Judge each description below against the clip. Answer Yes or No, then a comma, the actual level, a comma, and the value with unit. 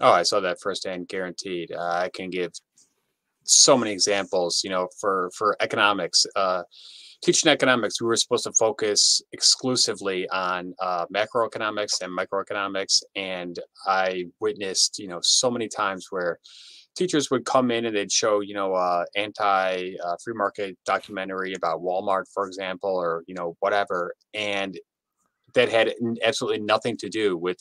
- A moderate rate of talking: Yes, average, 160 wpm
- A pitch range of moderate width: Yes, average, 4.0 semitones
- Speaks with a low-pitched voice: Yes, very low, 95 Hz